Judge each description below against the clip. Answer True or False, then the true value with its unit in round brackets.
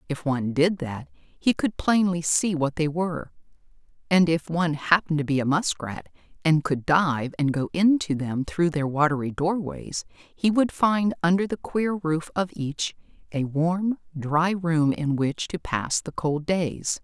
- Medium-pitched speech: True (160 Hz)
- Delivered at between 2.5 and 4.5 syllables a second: True (4.1 syllables/s)